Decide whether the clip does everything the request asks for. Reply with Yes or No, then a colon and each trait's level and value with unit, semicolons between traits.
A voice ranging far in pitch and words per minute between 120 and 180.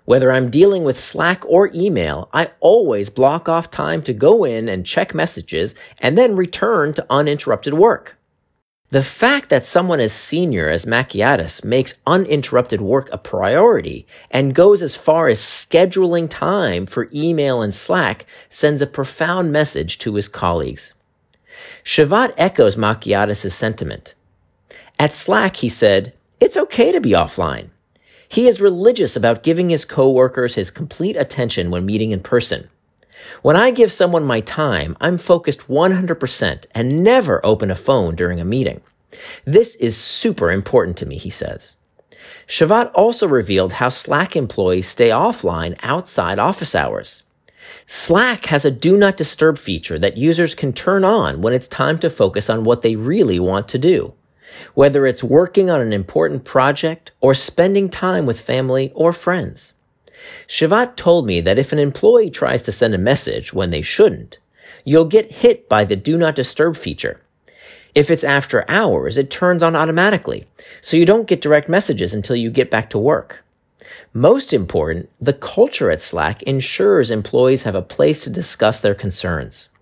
Yes: wide, 7.0 semitones; average, 160 wpm